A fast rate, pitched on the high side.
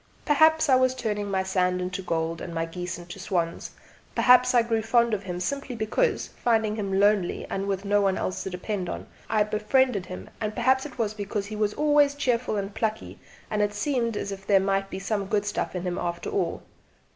Yes: fast, 215 wpm; high, 205 Hz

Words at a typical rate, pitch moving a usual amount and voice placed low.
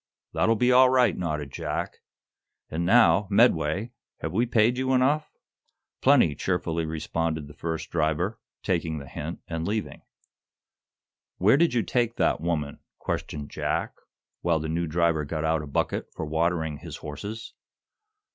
No: average, 145 wpm; wide, 6.2 semitones; very low, 85 Hz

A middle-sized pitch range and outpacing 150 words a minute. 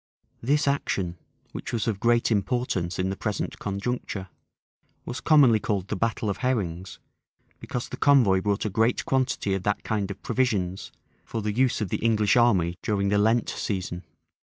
Yes: average, 3.8 semitones; average, 170 wpm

